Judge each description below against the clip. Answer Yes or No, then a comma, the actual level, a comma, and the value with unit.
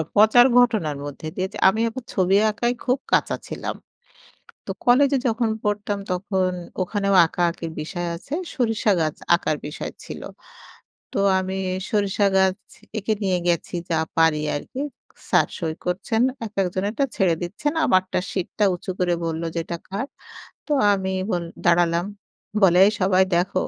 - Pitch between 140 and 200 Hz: Yes, high, 190 Hz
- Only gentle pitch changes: No, average, 3.5 semitones